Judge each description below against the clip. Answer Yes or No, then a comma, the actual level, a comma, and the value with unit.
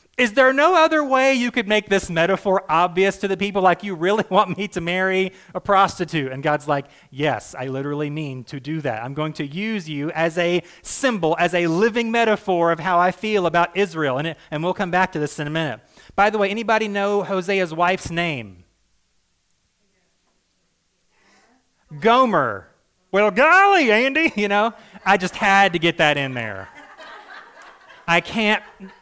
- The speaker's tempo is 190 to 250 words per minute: No, average, 180 wpm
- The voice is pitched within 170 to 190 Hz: Yes, medium, 185 Hz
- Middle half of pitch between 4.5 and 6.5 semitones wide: Yes, average, 4.9 semitones